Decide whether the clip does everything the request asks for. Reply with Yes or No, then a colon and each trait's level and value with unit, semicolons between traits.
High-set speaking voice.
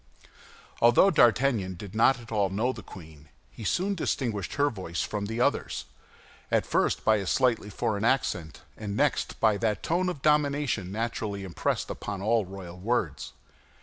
No: low, 110 Hz